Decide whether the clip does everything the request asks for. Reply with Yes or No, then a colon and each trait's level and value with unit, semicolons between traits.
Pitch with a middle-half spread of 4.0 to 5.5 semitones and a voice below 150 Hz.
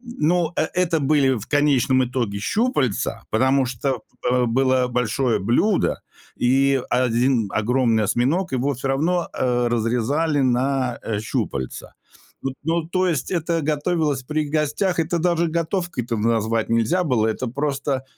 Yes: average, 4.7 semitones; low, 135 Hz